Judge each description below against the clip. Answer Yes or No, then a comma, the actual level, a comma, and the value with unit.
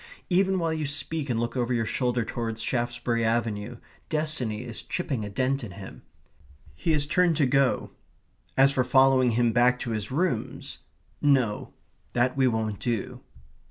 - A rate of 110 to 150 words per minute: No, average, 160 wpm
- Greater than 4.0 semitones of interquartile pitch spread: No, average, 3.2 semitones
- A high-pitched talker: No, low, 125 Hz